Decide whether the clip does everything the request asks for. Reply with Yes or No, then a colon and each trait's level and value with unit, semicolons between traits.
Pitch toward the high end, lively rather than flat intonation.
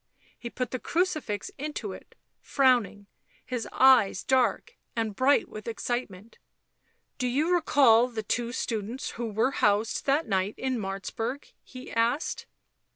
No: high, 240 Hz; average, 3.4 semitones